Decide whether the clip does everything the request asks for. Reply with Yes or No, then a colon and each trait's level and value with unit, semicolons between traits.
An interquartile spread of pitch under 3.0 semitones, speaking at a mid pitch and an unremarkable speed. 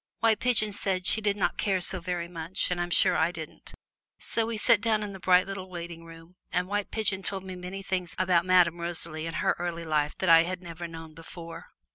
No: narrow, 2.5 semitones; medium, 180 Hz; fast, 225 wpm